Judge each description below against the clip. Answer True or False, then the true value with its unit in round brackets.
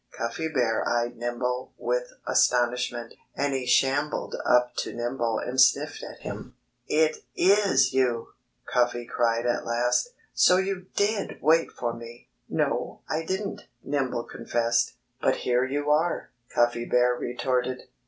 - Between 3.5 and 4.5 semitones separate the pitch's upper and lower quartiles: True (4.1 semitones)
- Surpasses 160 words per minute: False (135 wpm)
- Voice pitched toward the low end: True (125 Hz)